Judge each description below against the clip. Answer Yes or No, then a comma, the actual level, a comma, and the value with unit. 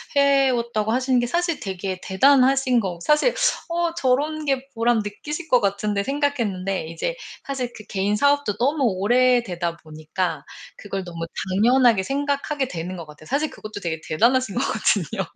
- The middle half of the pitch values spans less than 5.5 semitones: No, wide, 6.3 semitones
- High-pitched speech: Yes, high, 235 Hz